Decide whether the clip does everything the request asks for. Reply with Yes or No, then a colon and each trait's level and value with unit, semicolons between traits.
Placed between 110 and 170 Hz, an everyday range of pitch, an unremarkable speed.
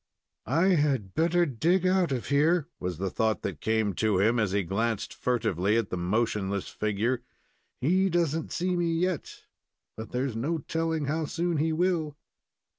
No: low, 135 Hz; wide, 7.5 semitones; average, 170 wpm